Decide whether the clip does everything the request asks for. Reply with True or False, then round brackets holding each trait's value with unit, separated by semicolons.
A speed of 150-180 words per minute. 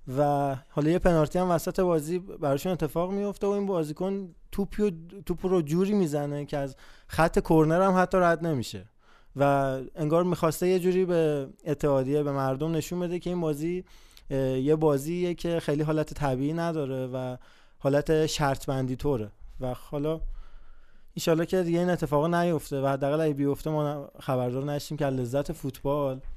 True (155 wpm)